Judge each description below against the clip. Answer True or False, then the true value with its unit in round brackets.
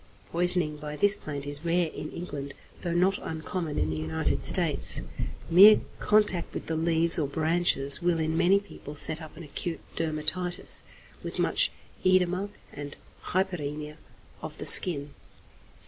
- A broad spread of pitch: False (3.1 semitones)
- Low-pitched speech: False (165 Hz)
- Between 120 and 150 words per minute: True (145 wpm)